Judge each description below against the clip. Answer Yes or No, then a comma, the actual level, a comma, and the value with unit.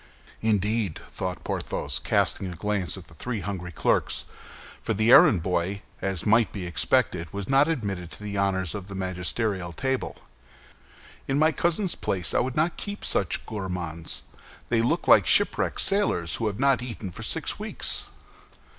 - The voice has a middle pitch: No, low, 100 Hz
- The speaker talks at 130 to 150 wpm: No, average, 160 wpm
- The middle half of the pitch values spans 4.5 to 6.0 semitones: Yes, average, 5.0 semitones